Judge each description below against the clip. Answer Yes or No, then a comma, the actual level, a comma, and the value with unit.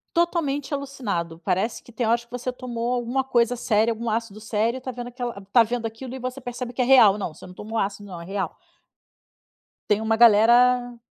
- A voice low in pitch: No, high, 235 Hz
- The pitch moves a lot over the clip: No, average, 2.7 semitones